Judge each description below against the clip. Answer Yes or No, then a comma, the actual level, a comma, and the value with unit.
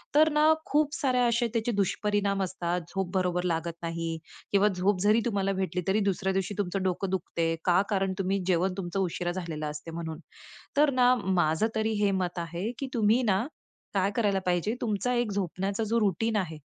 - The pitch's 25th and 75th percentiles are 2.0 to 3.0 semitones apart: No, average, 3.4 semitones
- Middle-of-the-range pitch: No, high, 195 Hz